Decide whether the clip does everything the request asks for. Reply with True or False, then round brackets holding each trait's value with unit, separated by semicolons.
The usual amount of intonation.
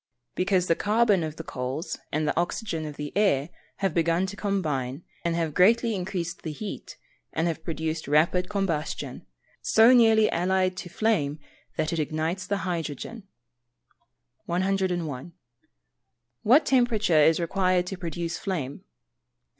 True (3.8 semitones)